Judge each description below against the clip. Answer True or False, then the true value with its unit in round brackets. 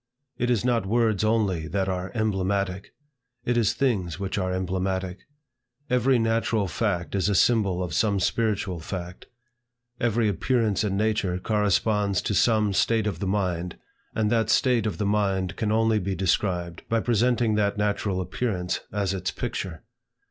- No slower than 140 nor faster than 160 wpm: True (155 wpm)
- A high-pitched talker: False (100 Hz)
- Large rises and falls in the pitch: False (3.1 semitones)